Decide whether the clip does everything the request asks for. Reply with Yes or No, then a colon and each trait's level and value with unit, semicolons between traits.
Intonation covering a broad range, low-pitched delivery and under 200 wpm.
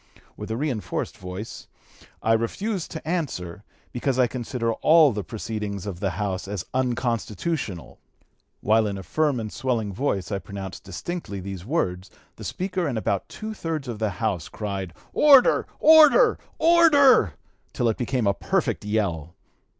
Yes: wide, 7.7 semitones; low, 110 Hz; average, 150 wpm